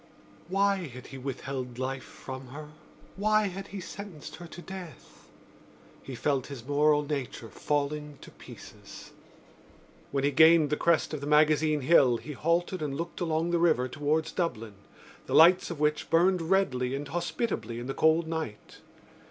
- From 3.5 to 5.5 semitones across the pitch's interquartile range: Yes, average, 4.0 semitones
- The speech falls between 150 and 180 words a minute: Yes, average, 160 wpm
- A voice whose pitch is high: No, medium, 150 Hz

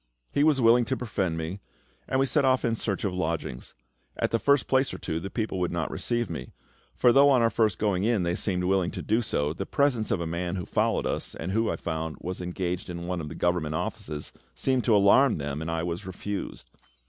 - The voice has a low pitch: Yes, very low, 95 Hz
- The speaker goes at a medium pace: No, fast, 235 wpm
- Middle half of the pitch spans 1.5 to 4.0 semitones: No, wide, 5.5 semitones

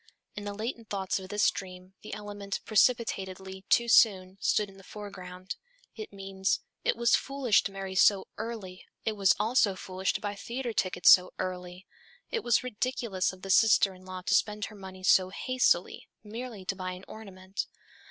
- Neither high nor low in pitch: No, high, 195 Hz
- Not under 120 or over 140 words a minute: No, average, 180 wpm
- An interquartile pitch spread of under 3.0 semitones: Yes, narrow, 2.6 semitones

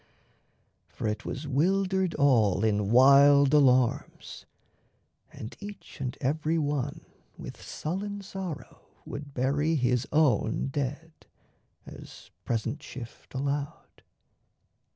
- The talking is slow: Yes, slow, 100 wpm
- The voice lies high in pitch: No, medium, 140 Hz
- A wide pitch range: No, average, 3.8 semitones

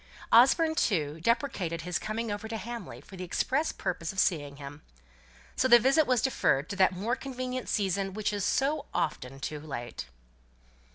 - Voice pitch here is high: Yes, high, 205 Hz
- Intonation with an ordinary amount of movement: No, wide, 7.3 semitones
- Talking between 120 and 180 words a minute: Yes, average, 170 wpm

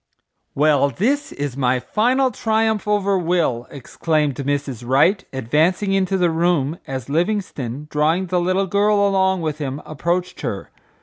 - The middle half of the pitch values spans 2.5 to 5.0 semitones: No, wide, 5.6 semitones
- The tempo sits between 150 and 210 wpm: No, average, 140 wpm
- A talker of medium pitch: Yes, medium, 170 Hz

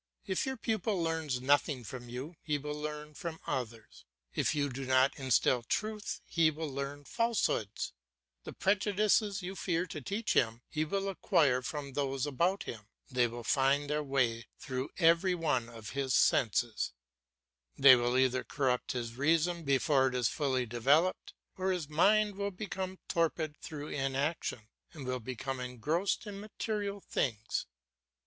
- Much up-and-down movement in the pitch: Yes, wide, 5.7 semitones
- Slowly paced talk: No, average, 155 wpm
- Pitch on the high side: No, medium, 145 Hz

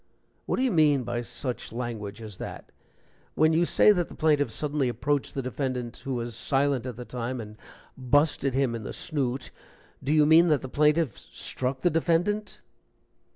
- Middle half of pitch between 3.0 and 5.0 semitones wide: Yes, average, 4.1 semitones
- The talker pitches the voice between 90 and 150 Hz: Yes, low, 135 Hz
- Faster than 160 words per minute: Yes, average, 180 wpm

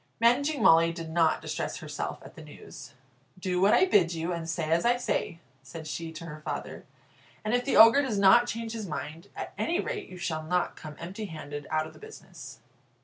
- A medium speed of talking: No, fast, 210 wpm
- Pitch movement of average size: No, wide, 6.1 semitones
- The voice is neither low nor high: Yes, medium, 175 Hz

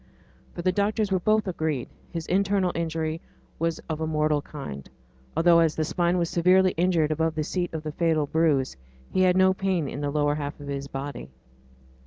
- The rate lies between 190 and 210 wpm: Yes, average, 195 wpm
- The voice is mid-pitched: Yes, medium, 165 Hz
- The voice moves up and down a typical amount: Yes, average, 3.2 semitones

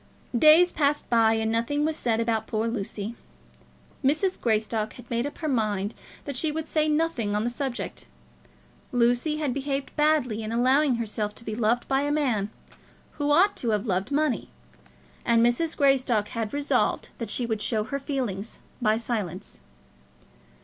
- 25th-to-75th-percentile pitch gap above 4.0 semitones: Yes, average, 4.7 semitones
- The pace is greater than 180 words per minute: No, average, 165 wpm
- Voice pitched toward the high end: Yes, high, 240 Hz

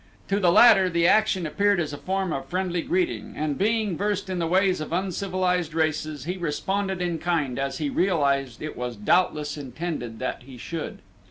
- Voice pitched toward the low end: No, medium, 175 Hz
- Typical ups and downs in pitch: Yes, average, 4.2 semitones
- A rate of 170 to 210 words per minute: Yes, average, 185 wpm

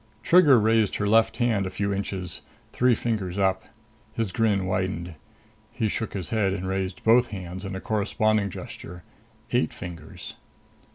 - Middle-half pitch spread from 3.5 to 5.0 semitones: No, average, 3.0 semitones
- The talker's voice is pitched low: Yes, low, 100 Hz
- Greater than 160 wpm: No, average, 155 wpm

